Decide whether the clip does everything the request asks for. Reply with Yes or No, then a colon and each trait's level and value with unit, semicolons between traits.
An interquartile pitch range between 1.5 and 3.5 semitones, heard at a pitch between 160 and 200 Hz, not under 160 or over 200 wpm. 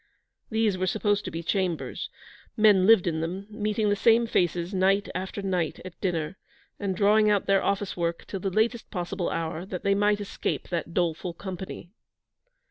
Yes: average, 2.8 semitones; high, 190 Hz; average, 175 wpm